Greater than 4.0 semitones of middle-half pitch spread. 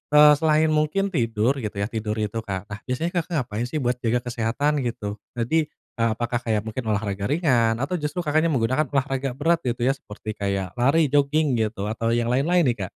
Yes: average, 5.2 semitones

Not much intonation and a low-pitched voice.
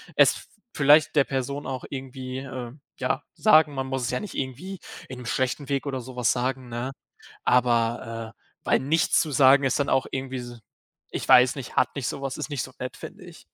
Yes: narrow, 1.9 semitones; low, 130 Hz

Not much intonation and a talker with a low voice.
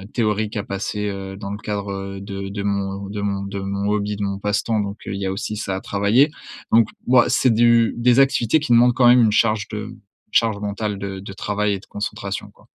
Yes: narrow, 2.3 semitones; low, 105 Hz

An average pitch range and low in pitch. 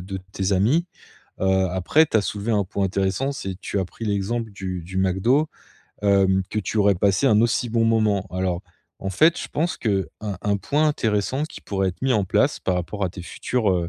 Yes: average, 3.2 semitones; low, 100 Hz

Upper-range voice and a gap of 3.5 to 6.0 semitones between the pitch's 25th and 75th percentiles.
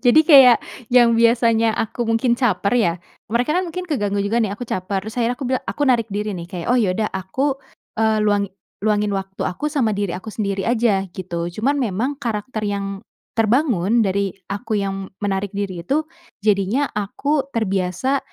Yes: high, 215 Hz; average, 3.8 semitones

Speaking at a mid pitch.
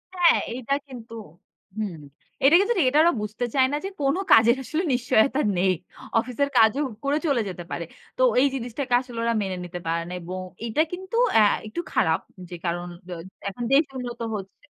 No: high, 240 Hz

